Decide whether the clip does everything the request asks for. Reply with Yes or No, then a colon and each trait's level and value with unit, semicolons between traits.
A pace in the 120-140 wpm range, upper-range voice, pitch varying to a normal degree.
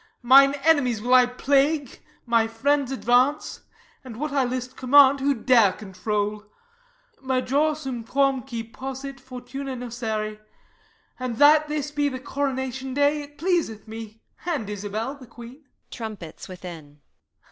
Yes: slow, 135 wpm; very high, 255 Hz; average, 3.7 semitones